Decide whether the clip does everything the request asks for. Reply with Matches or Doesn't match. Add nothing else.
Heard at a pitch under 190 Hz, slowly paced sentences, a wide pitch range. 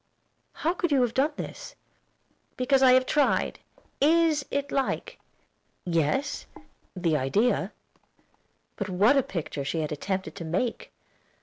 Doesn't match